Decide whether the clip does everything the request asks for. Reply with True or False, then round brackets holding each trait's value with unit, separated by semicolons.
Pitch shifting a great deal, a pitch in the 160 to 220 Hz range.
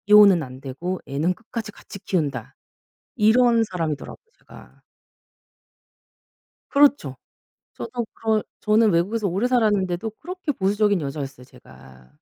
True (6.5 semitones; 200 Hz)